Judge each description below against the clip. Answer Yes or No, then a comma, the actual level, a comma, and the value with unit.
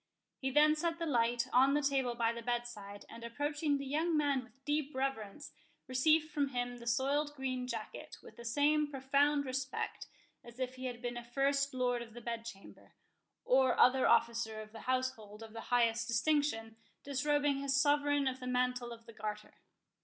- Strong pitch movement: No, average, 3.2 semitones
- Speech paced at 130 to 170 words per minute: No, average, 185 wpm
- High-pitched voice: Yes, very high, 255 Hz